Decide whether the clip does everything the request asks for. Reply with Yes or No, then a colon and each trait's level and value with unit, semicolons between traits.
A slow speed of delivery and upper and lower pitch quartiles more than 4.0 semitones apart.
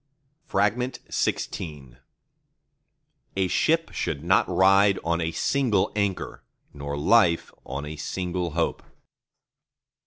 Yes: slow, 95 wpm; average, 4.4 semitones